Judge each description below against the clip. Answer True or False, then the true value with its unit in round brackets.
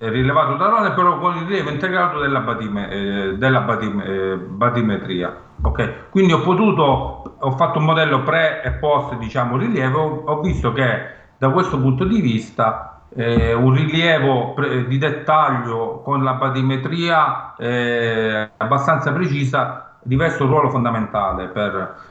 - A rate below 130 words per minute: False (145 wpm)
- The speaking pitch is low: True (130 Hz)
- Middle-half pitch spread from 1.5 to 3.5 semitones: False (5.3 semitones)